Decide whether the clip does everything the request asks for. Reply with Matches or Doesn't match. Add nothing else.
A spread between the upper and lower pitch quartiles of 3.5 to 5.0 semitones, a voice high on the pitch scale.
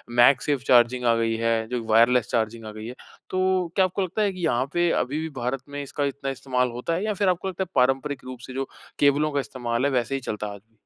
Doesn't match